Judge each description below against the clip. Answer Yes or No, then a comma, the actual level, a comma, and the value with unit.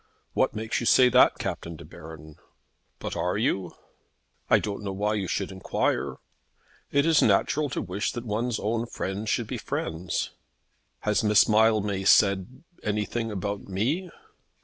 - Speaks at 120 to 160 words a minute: Yes, average, 150 wpm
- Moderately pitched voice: No, low, 105 Hz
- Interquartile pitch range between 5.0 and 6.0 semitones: No, average, 3.3 semitones